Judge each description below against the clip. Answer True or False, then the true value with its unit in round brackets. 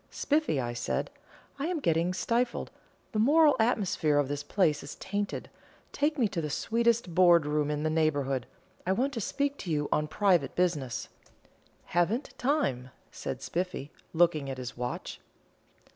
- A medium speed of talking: True (160 wpm)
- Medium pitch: True (175 Hz)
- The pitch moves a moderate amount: False (7.9 semitones)